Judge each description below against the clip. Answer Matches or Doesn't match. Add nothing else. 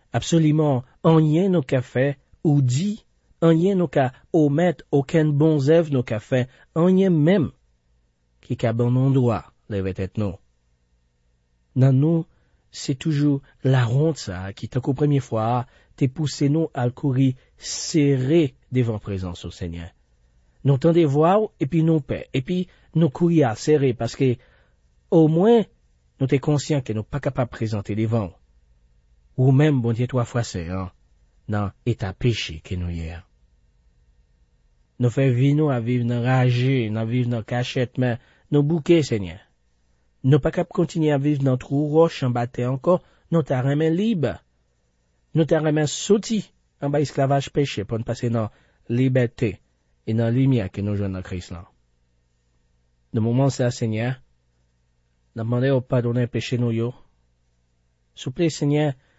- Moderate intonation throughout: Doesn't match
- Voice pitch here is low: Matches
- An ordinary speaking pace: Matches